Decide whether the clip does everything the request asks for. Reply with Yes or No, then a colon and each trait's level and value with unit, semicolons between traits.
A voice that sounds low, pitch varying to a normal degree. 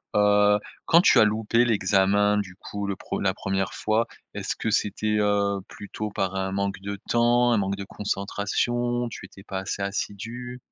No: low, 105 Hz; narrow, 2.2 semitones